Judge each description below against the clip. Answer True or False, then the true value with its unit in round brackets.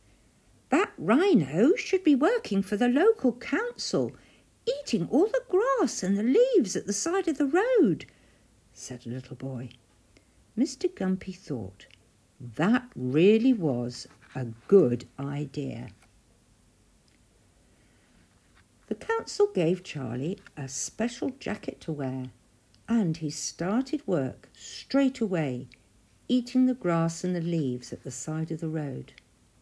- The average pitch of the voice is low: False (165 Hz)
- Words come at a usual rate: False (125 wpm)